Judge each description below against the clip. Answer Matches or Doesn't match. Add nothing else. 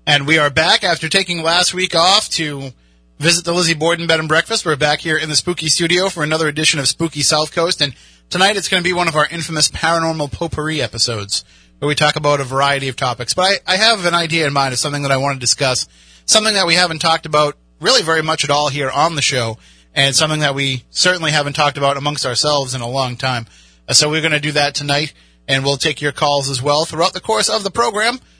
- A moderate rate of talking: Doesn't match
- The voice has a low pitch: Doesn't match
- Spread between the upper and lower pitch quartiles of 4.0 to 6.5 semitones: Doesn't match